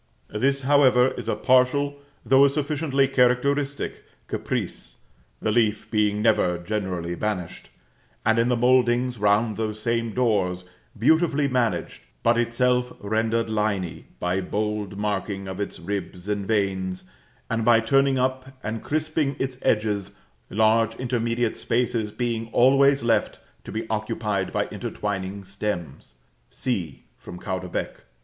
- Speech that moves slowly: Yes, slow, 130 wpm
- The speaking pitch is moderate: No, low, 115 Hz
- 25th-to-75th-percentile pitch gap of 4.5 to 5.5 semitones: No, average, 3.8 semitones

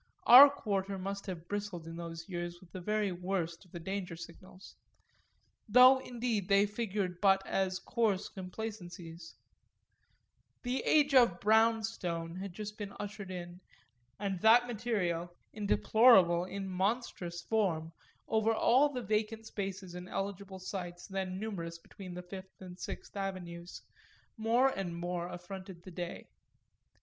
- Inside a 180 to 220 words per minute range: No, average, 140 wpm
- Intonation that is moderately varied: Yes, average, 3.4 semitones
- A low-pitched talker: No, high, 195 Hz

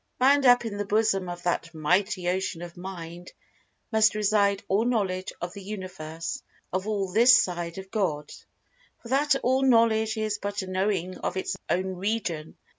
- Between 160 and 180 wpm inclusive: Yes, average, 165 wpm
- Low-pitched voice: No, high, 195 Hz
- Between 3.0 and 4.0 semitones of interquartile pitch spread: Yes, average, 3.5 semitones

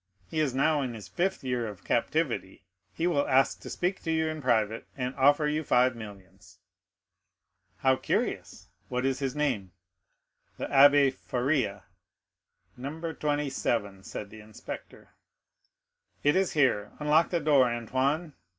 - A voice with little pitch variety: No, average, 4.3 semitones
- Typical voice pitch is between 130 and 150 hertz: Yes, low, 135 Hz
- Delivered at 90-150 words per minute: Yes, average, 140 wpm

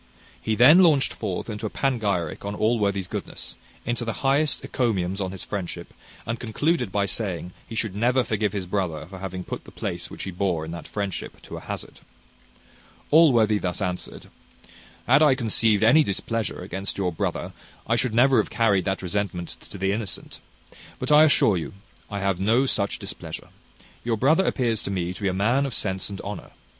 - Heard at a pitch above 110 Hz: No, low, 105 Hz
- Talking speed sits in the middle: Yes, average, 190 wpm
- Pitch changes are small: No, average, 4.0 semitones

